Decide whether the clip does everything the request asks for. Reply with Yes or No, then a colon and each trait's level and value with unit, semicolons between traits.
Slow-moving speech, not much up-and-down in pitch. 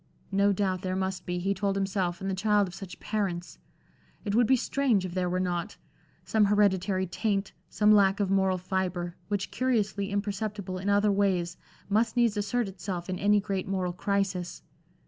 No: average, 180 wpm; narrow, 1.9 semitones